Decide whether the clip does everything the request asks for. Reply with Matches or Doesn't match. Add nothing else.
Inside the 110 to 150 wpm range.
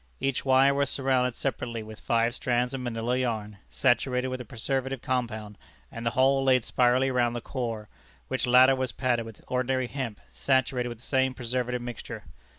Doesn't match